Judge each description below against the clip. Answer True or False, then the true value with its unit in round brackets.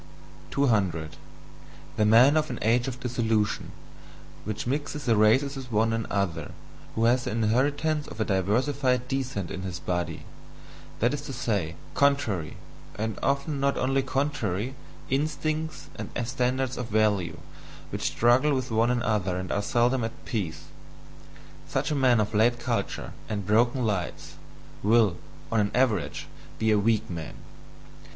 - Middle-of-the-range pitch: False (120 Hz)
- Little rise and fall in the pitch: False (4.2 semitones)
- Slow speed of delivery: False (145 wpm)